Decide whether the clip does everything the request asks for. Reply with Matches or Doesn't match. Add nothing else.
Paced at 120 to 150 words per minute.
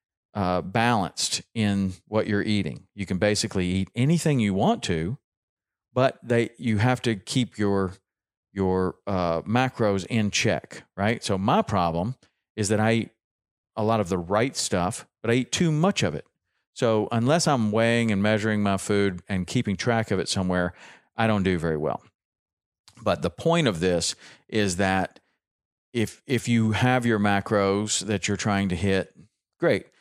Doesn't match